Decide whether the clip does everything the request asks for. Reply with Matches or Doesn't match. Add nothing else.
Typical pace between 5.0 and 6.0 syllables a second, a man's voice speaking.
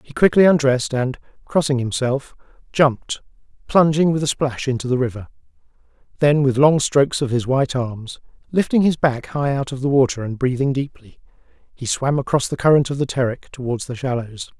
Matches